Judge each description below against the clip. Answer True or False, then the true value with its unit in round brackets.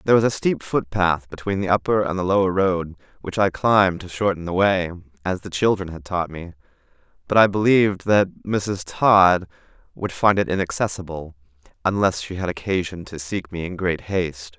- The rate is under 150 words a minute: False (185 wpm)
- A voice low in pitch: True (90 Hz)